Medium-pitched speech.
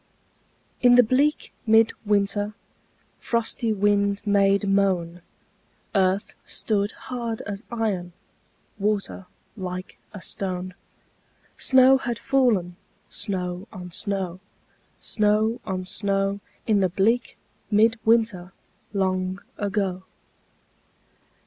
No: high, 200 Hz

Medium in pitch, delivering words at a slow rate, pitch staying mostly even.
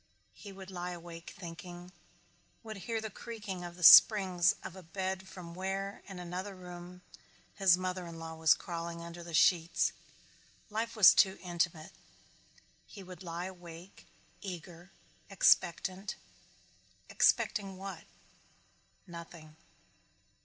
Yes: medium, 180 Hz; slow, 125 wpm; narrow, 2.0 semitones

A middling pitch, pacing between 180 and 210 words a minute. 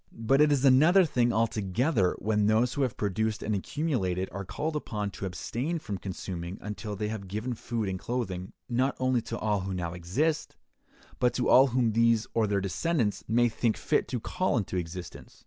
No: low, 110 Hz; average, 190 wpm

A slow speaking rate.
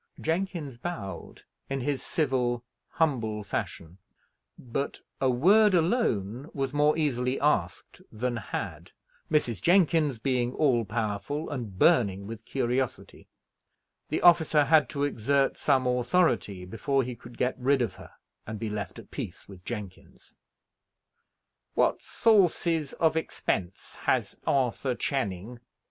Yes: slow, 125 wpm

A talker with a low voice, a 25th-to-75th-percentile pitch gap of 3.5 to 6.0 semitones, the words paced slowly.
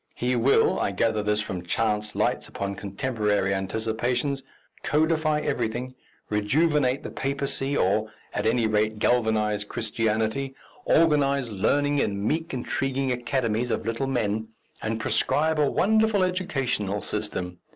Yes: low, 120 Hz; average, 4.7 semitones; slow, 125 wpm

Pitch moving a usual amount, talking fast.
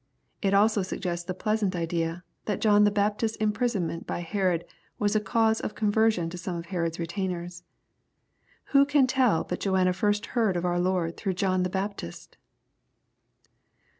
No: average, 3.3 semitones; average, 160 wpm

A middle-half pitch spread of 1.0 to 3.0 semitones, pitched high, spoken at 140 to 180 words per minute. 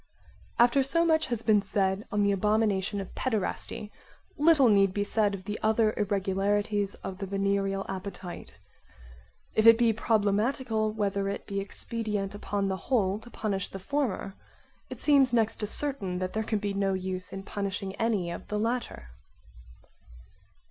Yes: narrow, 2.4 semitones; high, 205 Hz; average, 160 wpm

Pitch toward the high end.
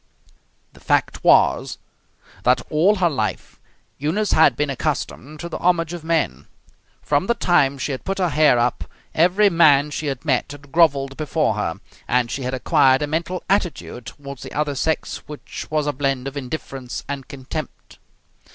No: medium, 145 Hz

